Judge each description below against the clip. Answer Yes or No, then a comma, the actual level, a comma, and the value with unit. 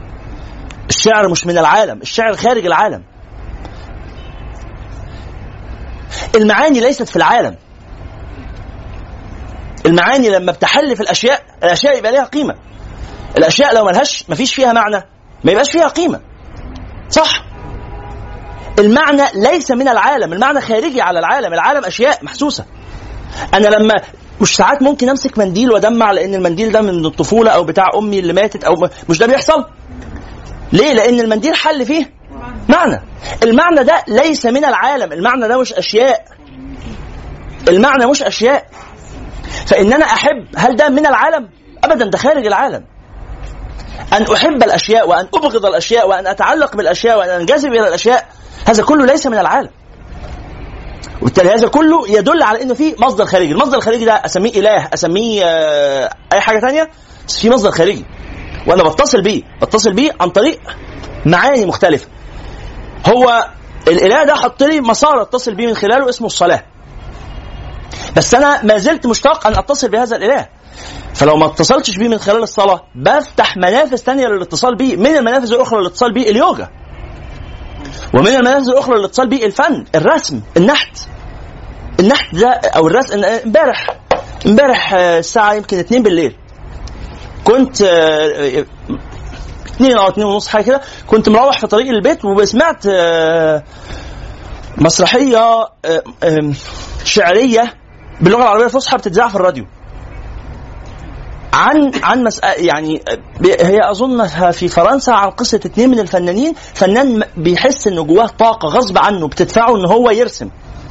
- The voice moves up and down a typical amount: No, wide, 7.3 semitones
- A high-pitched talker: Yes, high, 215 Hz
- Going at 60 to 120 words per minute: No, fast, 135 wpm